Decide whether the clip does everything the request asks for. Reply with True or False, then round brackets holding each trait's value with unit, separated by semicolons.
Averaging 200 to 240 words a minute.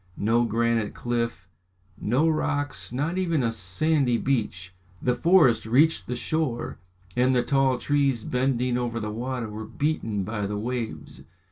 False (145 wpm)